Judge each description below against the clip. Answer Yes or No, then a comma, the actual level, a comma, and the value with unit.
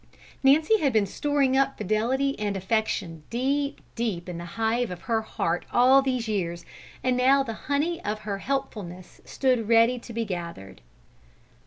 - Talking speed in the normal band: Yes, average, 160 wpm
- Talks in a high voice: Yes, high, 230 Hz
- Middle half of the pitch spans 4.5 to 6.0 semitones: Yes, wide, 5.4 semitones